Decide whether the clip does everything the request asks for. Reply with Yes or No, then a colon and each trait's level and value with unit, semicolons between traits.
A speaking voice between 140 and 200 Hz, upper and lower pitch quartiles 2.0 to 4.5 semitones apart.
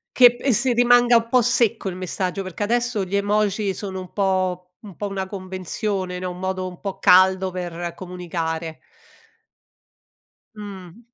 Yes: high, 190 Hz; narrow, 2.6 semitones